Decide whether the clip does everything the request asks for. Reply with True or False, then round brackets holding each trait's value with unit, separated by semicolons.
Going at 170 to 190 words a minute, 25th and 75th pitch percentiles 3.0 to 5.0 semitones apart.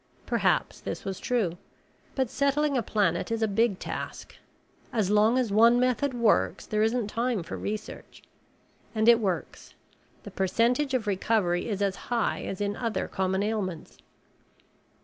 False (150 wpm; 3.5 semitones)